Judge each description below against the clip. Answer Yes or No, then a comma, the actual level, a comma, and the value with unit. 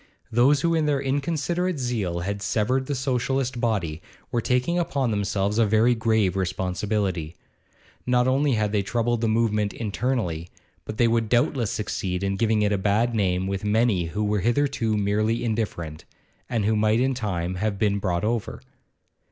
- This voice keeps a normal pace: Yes, average, 170 wpm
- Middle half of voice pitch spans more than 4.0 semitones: No, average, 3.6 semitones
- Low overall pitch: Yes, low, 110 Hz